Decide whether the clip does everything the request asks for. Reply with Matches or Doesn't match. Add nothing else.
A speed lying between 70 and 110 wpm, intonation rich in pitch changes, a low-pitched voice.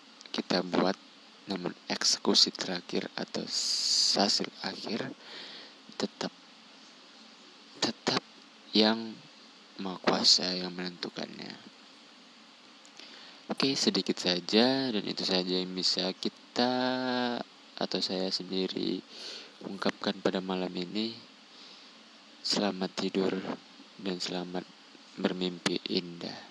Matches